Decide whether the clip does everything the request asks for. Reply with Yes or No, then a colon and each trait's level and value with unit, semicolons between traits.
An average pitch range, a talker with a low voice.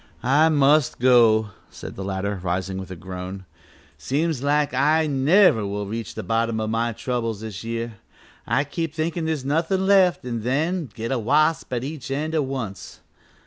No: wide, 5.9 semitones; low, 125 Hz